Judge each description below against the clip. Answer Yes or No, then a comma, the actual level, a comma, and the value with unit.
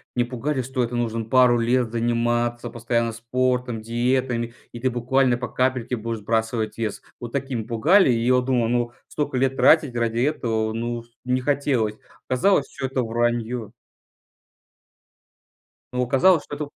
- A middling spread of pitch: No, narrow, 1.8 semitones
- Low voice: Yes, low, 120 Hz